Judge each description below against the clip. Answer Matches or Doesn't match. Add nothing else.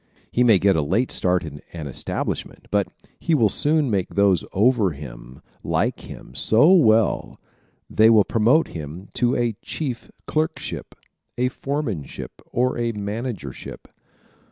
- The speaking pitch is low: Matches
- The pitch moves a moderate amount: Doesn't match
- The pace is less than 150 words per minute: Matches